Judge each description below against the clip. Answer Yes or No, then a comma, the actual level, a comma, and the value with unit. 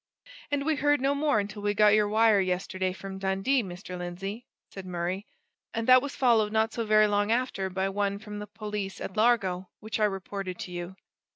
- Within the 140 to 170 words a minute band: No, average, 200 wpm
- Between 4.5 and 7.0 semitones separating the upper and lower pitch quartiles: No, average, 2.7 semitones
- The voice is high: Yes, high, 205 Hz